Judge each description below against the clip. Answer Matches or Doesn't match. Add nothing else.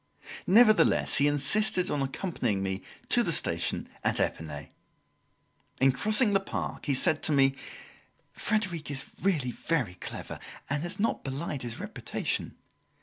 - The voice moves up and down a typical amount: Doesn't match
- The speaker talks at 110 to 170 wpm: Matches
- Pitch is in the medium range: Matches